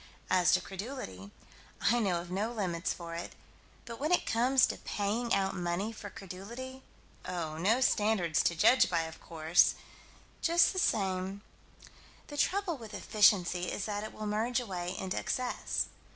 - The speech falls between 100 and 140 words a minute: No, average, 160 wpm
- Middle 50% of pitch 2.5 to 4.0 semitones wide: No, average, 4.9 semitones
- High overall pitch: Yes, high, 200 Hz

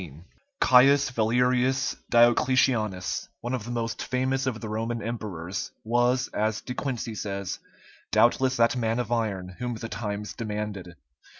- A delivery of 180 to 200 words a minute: No, average, 140 wpm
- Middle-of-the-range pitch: No, low, 115 Hz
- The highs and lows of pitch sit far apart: No, average, 3.0 semitones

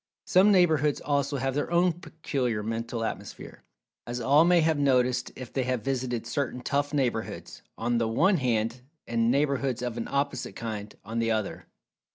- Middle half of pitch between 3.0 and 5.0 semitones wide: Yes, average, 3.7 semitones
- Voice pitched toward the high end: No, low, 130 Hz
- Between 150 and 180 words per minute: Yes, average, 175 wpm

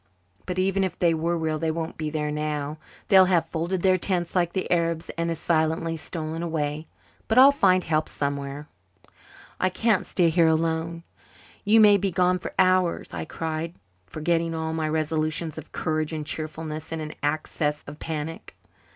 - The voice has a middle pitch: Yes, medium, 165 Hz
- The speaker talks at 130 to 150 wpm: No, average, 175 wpm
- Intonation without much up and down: Yes, narrow, 2.2 semitones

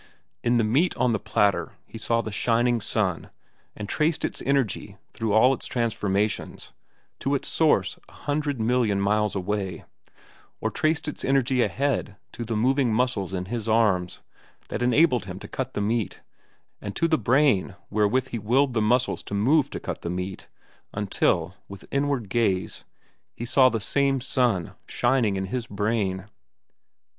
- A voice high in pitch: No, low, 115 Hz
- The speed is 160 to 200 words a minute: Yes, average, 165 wpm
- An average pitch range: Yes, average, 4.2 semitones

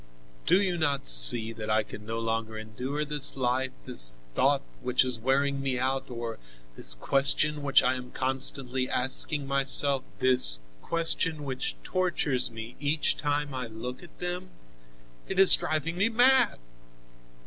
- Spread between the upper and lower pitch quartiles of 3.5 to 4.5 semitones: Yes, average, 3.9 semitones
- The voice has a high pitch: No, low, 135 Hz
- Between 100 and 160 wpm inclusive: Yes, average, 150 wpm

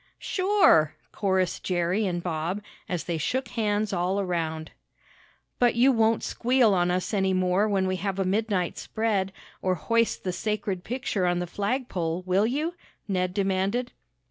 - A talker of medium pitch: No, high, 195 Hz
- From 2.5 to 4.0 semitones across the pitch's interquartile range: Yes, average, 3.6 semitones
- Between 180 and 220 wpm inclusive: No, average, 155 wpm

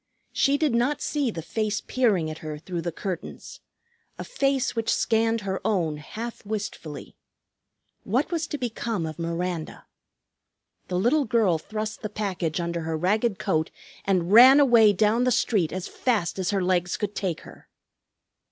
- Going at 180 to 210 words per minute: No, average, 160 wpm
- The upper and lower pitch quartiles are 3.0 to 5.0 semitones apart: No, wide, 5.4 semitones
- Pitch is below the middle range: No, high, 205 Hz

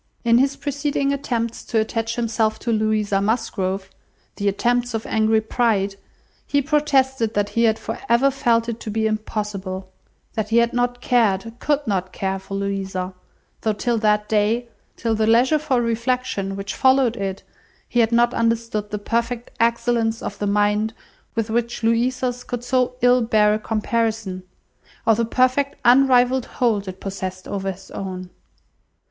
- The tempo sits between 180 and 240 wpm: No, average, 160 wpm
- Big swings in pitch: No, average, 2.9 semitones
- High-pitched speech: Yes, high, 225 Hz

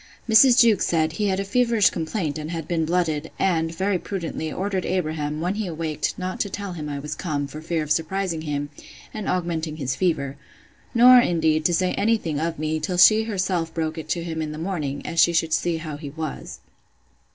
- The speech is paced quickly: Yes, fast, 210 wpm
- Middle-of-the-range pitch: Yes, medium, 165 Hz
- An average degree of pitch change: Yes, average, 3.3 semitones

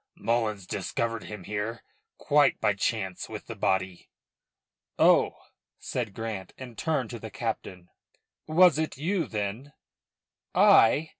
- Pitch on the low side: Yes, low, 115 Hz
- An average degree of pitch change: No, wide, 5.7 semitones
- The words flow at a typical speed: No, slow, 130 wpm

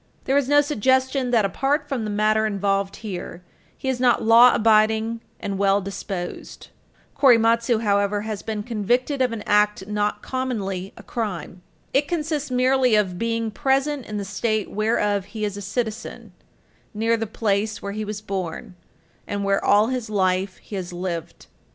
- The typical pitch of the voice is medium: No, high, 215 Hz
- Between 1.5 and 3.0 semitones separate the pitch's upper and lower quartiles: No, average, 3.6 semitones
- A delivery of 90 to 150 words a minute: No, average, 165 wpm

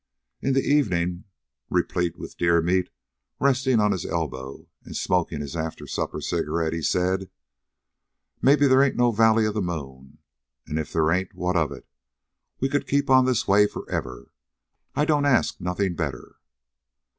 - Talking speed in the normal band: Yes, average, 160 wpm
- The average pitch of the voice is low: Yes, very low, 90 Hz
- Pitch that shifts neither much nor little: No, wide, 7.5 semitones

